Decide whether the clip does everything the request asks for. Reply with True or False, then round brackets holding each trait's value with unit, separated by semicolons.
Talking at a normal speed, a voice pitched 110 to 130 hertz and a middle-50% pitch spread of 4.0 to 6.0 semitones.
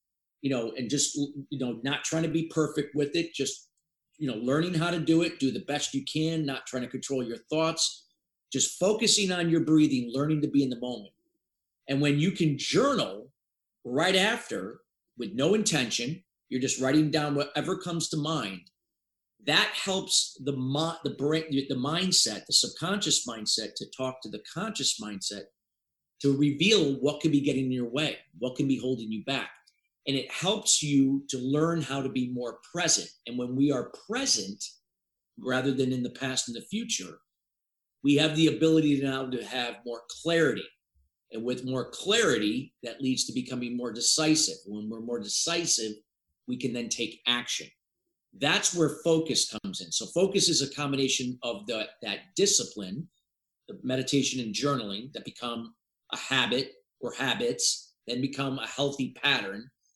False (175 wpm; 140 Hz; 4.3 semitones)